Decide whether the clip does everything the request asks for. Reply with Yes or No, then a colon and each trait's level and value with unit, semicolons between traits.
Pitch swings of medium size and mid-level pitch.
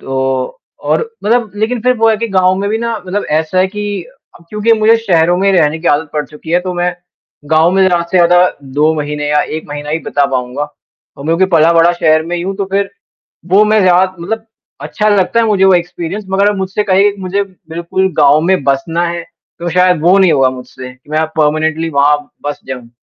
Yes: average, 4.2 semitones; medium, 175 Hz